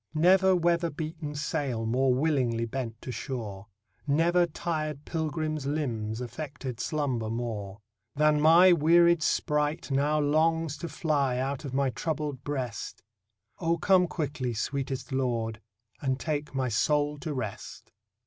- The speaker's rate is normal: No, slow, 130 wpm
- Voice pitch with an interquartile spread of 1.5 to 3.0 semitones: No, average, 3.8 semitones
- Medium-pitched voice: Yes, medium, 145 Hz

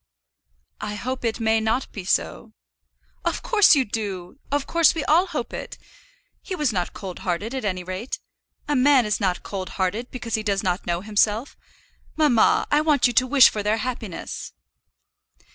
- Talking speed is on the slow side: No, average, 180 wpm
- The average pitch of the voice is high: Yes, high, 225 Hz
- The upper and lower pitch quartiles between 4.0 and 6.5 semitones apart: Yes, average, 5.3 semitones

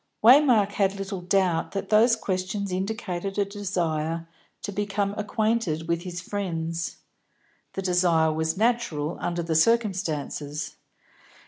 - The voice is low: No, high, 190 Hz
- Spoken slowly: Yes, slow, 120 wpm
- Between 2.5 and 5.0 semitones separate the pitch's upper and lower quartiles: Yes, average, 3.6 semitones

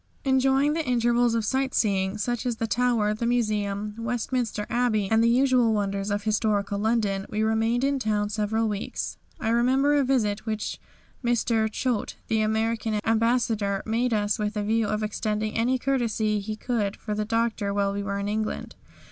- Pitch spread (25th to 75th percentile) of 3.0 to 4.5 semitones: No, narrow, 2.4 semitones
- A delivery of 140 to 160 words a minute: No, average, 175 wpm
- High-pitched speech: Yes, high, 220 Hz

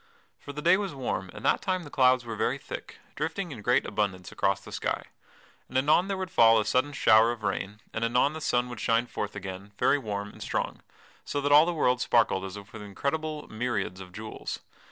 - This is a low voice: Yes, low, 120 Hz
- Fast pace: Yes, fast, 215 wpm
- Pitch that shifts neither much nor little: No, wide, 5.7 semitones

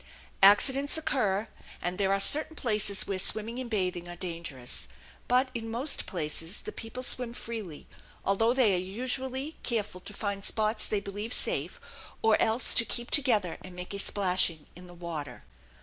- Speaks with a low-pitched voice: No, high, 210 Hz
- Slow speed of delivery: No, average, 165 wpm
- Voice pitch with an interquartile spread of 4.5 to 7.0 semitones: Yes, average, 4.8 semitones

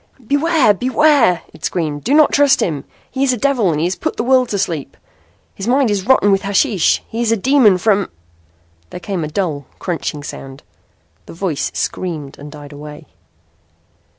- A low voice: No, high, 195 Hz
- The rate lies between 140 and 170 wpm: No, average, 180 wpm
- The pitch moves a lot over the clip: Yes, wide, 8.8 semitones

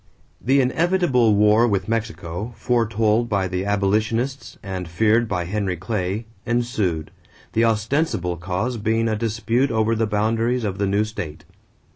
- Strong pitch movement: No, average, 2.9 semitones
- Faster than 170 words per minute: No, average, 145 wpm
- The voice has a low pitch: Yes, low, 110 Hz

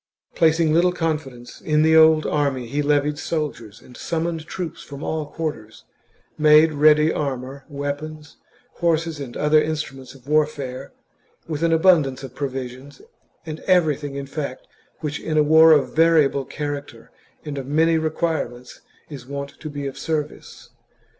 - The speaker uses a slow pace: No, average, 155 wpm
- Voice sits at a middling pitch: Yes, medium, 150 Hz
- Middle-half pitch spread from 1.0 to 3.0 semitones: Yes, narrow, 2.4 semitones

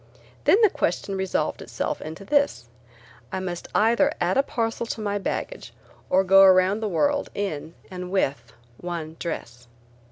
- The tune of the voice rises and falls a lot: No, average, 4.1 semitones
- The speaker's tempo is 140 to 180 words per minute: Yes, average, 155 wpm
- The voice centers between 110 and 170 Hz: No, high, 190 Hz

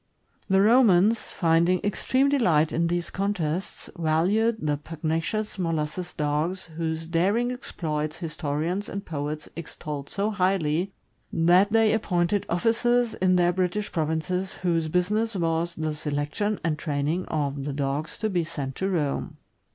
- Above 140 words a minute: No, slow, 135 wpm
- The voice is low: No, medium, 170 Hz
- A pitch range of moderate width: Yes, average, 4.2 semitones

